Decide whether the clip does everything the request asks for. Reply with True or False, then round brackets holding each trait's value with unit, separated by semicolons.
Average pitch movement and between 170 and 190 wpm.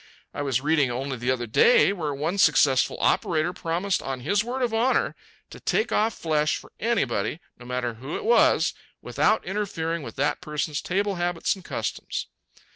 False (6.8 semitones; 175 wpm)